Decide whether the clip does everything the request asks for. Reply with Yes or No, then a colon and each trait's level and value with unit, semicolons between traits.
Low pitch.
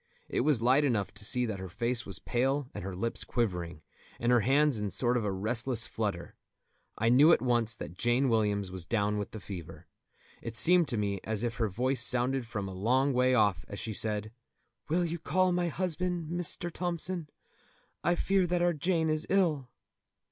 Yes: low, 120 Hz